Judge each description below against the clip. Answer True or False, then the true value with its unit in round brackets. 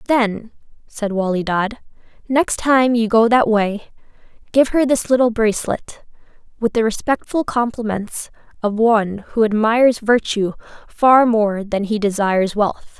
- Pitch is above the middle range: True (225 Hz)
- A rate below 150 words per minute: True (140 wpm)